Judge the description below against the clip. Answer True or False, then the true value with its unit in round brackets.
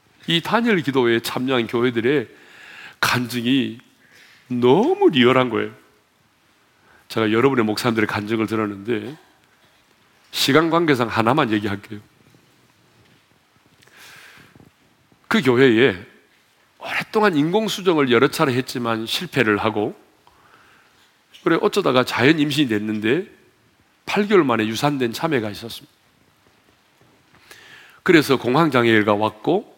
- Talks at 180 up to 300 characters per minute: True (240 characters per minute)